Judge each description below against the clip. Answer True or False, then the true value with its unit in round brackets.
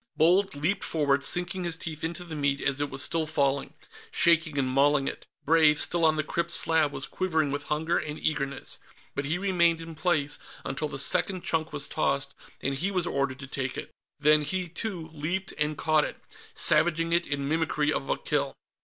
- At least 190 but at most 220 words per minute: True (200 wpm)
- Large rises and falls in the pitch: False (3.1 semitones)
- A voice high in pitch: False (155 Hz)